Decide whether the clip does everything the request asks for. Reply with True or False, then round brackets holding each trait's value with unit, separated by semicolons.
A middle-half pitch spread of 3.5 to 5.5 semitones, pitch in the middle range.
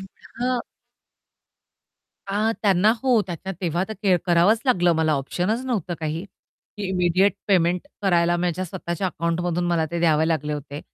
False (2.9 semitones; 175 Hz)